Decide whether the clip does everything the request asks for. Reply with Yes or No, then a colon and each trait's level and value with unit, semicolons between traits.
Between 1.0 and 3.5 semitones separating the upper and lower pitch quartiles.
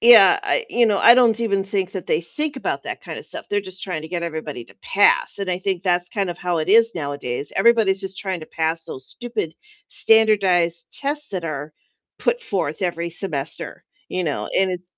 No: average, 4.8 semitones